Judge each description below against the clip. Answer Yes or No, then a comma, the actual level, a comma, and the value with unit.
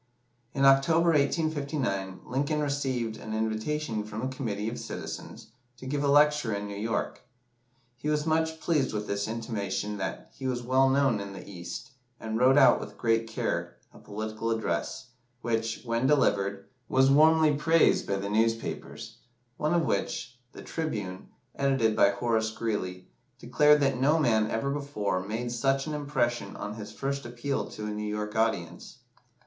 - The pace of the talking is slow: No, average, 165 wpm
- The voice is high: No, low, 120 Hz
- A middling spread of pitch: Yes, average, 4.7 semitones